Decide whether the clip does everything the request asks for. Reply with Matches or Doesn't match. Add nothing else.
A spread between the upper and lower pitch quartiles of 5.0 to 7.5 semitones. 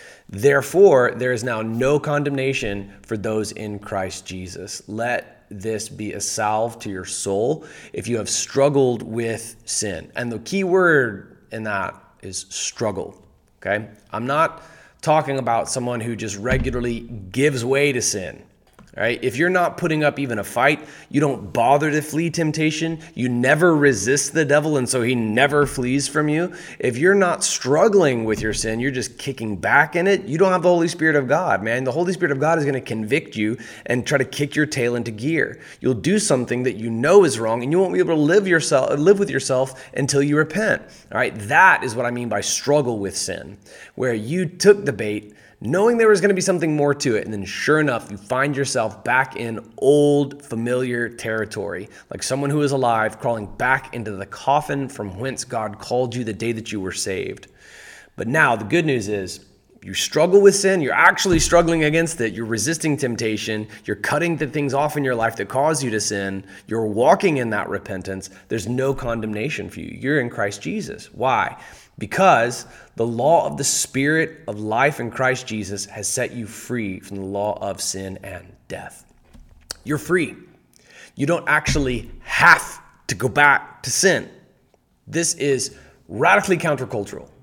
Matches